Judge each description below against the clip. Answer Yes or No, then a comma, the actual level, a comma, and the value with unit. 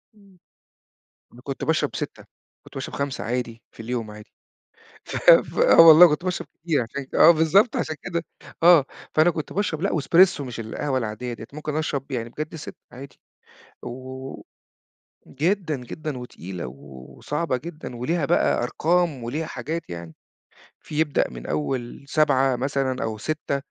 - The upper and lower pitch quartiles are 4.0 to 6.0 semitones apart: Yes, average, 4.7 semitones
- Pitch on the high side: No, medium, 140 Hz